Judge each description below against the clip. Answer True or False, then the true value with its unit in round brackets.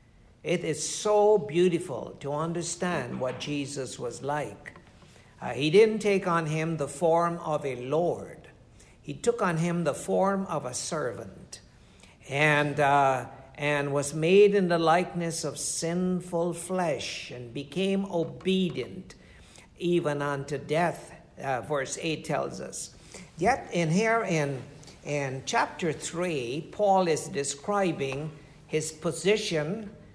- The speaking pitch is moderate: True (160 Hz)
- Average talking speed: False (125 wpm)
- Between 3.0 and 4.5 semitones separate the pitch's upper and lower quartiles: True (3.8 semitones)